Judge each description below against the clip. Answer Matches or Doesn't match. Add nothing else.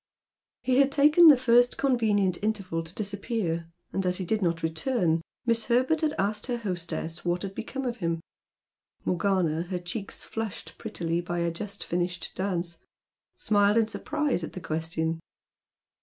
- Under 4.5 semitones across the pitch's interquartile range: Doesn't match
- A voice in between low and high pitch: Doesn't match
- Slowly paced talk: Doesn't match